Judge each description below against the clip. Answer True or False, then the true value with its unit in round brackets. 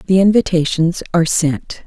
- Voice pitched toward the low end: False (175 Hz)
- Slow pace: True (130 wpm)